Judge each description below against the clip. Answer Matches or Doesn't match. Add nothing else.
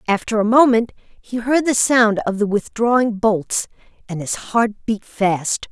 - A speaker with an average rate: Matches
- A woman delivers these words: Matches